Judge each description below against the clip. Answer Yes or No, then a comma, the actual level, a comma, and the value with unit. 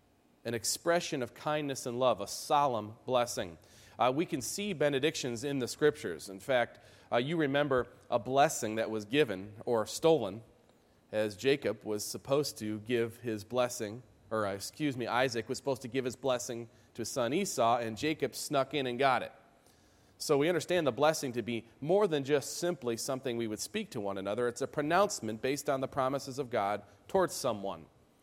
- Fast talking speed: No, average, 185 wpm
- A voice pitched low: Yes, low, 125 Hz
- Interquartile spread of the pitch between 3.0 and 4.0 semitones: No, average, 4.4 semitones